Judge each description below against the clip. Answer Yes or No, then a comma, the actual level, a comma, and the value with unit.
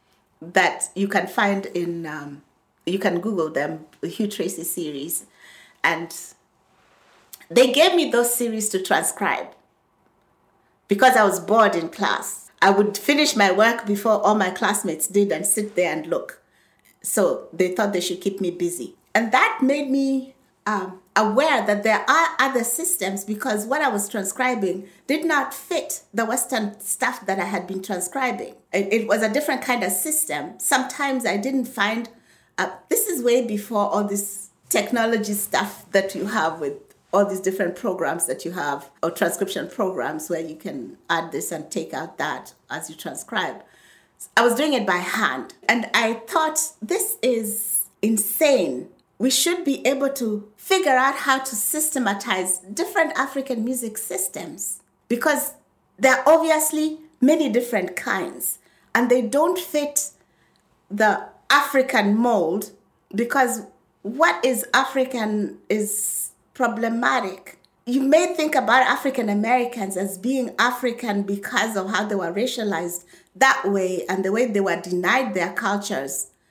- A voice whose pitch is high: Yes, high, 220 Hz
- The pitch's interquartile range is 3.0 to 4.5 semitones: No, average, 5.2 semitones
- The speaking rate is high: No, average, 150 wpm